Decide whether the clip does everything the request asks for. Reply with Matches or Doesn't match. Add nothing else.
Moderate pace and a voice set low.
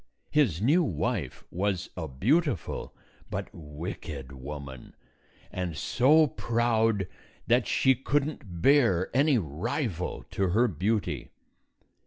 Doesn't match